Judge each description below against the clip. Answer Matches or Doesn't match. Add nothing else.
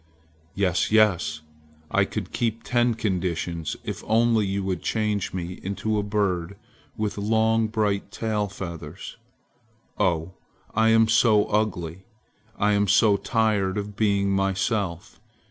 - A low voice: Matches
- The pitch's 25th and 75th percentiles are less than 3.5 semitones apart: Matches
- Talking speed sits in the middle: Doesn't match